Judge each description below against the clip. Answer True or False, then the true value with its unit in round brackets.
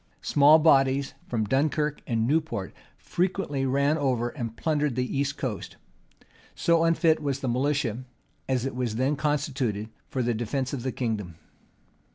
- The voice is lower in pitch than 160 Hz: True (135 Hz)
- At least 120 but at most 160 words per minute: True (150 wpm)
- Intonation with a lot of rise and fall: False (3.6 semitones)